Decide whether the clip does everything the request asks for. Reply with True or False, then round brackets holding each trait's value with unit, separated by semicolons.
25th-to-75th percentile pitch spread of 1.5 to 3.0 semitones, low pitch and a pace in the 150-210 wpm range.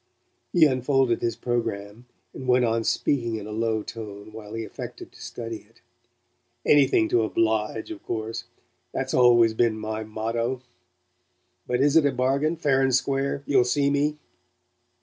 False (3.4 semitones; 120 Hz; 155 wpm)